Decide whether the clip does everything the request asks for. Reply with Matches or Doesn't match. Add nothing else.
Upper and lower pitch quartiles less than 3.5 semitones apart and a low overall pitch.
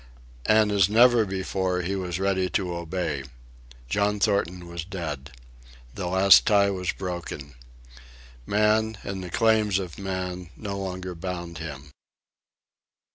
Matches